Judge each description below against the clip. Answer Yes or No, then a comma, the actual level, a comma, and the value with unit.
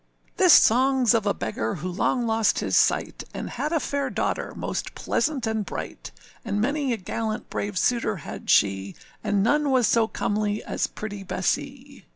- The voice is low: No, high, 220 Hz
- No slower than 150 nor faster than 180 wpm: Yes, average, 175 wpm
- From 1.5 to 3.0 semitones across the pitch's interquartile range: No, average, 4.3 semitones